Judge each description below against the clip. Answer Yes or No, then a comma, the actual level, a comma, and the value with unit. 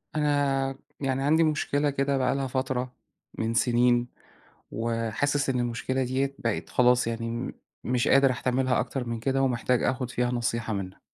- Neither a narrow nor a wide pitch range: No, narrow, 2.3 semitones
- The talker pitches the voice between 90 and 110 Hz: No, low, 125 Hz